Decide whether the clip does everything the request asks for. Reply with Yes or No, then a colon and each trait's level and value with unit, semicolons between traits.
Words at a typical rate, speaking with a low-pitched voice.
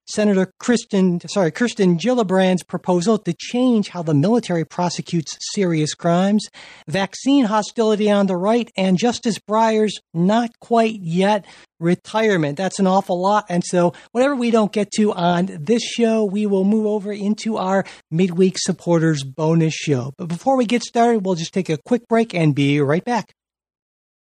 No: average, 160 wpm; high, 195 Hz